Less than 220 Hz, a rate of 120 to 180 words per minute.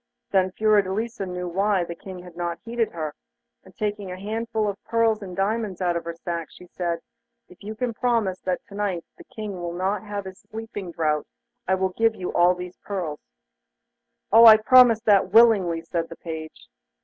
No: high, 190 Hz; average, 195 wpm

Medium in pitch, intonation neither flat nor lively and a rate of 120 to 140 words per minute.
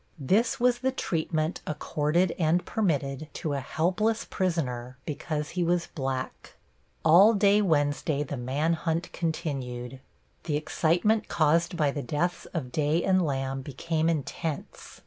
Yes: medium, 160 Hz; average, 3.7 semitones; slow, 135 wpm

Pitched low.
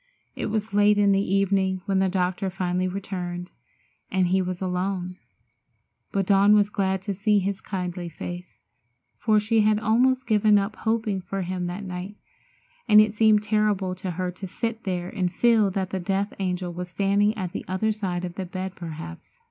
No: high, 195 Hz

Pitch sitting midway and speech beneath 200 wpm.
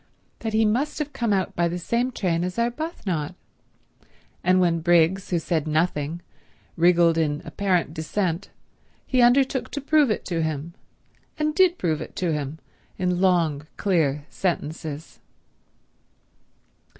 Yes: medium, 180 Hz; average, 140 wpm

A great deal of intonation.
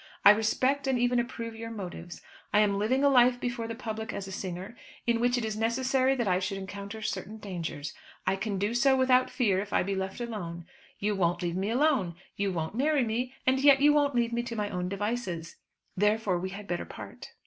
No: average, 4.2 semitones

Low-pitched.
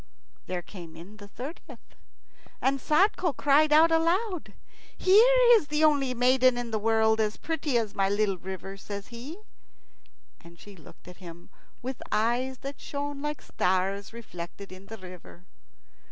No: high, 235 Hz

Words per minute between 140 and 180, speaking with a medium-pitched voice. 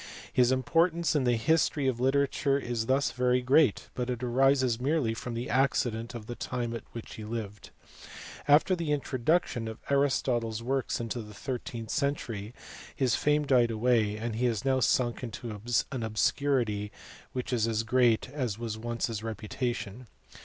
No: average, 170 wpm; low, 125 Hz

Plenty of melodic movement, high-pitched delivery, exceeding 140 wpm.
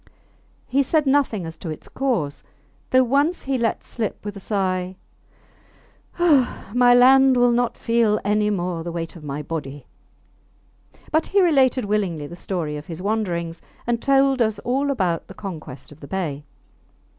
Yes: wide, 7.2 semitones; high, 210 Hz; average, 165 wpm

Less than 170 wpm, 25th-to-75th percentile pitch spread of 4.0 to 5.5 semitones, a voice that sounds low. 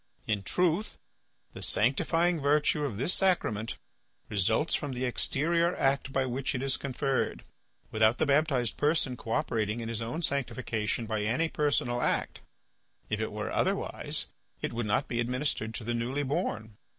Yes: average, 155 wpm; average, 4.3 semitones; low, 130 Hz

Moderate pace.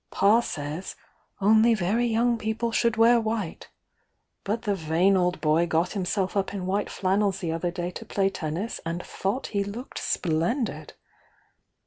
Yes: average, 155 wpm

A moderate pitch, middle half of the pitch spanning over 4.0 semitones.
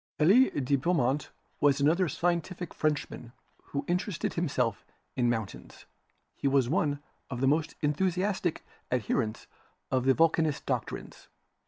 Yes: medium, 145 Hz; average, 4.6 semitones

